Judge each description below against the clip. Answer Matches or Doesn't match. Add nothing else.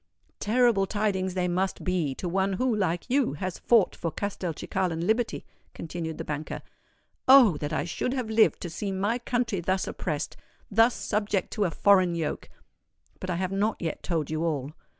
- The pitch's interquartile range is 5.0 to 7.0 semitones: Doesn't match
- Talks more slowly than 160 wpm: Doesn't match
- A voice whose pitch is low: Doesn't match